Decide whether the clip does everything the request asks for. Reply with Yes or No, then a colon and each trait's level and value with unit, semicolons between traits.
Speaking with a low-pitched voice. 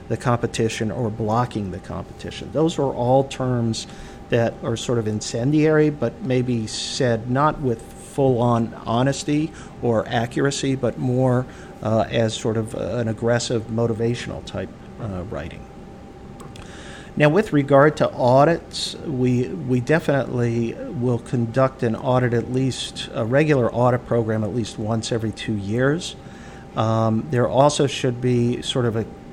Yes: low, 120 Hz